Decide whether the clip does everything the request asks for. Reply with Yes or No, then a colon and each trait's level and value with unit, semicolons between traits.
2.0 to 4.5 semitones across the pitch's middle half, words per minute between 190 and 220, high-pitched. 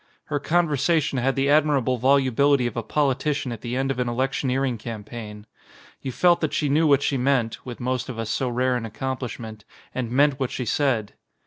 No: average, 2.9 semitones; average, 200 wpm; low, 130 Hz